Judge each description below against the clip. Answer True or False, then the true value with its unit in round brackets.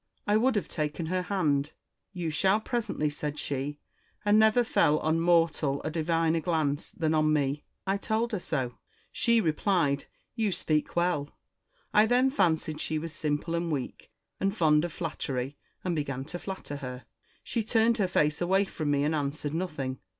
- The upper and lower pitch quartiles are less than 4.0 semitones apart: False (4.6 semitones)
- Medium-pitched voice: True (160 Hz)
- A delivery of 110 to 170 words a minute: False (180 wpm)